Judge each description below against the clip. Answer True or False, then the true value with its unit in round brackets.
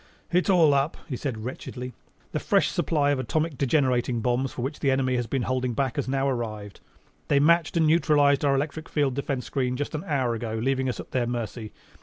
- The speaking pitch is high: False (135 Hz)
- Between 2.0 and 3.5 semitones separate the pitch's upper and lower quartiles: True (2.8 semitones)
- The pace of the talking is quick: True (210 wpm)